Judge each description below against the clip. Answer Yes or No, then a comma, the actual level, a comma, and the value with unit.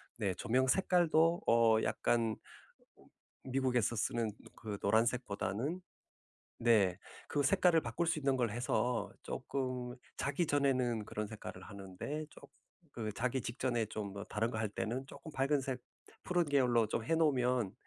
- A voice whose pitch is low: Yes, low, 125 Hz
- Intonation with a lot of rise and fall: No, average, 4.0 semitones